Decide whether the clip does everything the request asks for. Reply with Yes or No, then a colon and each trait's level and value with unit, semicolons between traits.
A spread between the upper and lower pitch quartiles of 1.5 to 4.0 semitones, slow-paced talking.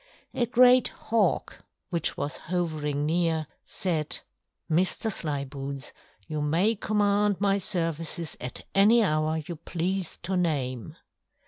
No: average, 4.5 semitones; slow, 115 wpm